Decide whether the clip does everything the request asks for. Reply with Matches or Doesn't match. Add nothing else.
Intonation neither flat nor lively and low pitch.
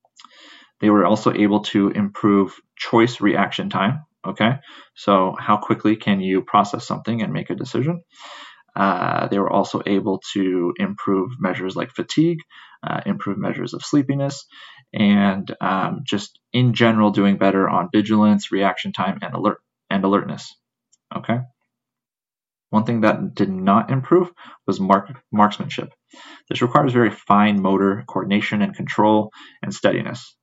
Matches